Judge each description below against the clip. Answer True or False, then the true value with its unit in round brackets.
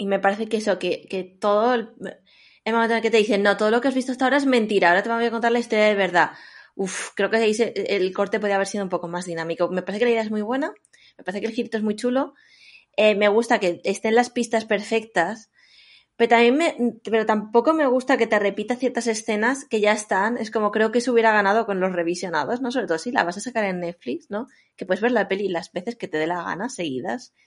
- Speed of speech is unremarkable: False (265 wpm)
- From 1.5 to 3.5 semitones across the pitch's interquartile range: True (3.2 semitones)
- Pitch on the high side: True (220 Hz)